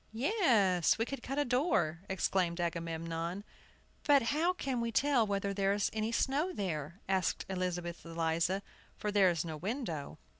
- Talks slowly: No, average, 155 wpm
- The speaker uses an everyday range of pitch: No, wide, 6.0 semitones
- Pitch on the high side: Yes, high, 195 Hz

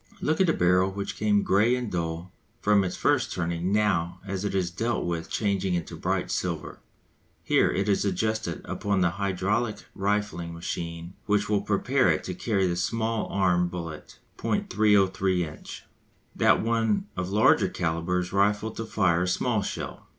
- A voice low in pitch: Yes, very low, 95 Hz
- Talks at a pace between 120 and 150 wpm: No, average, 165 wpm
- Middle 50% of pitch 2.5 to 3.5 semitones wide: Yes, average, 3.0 semitones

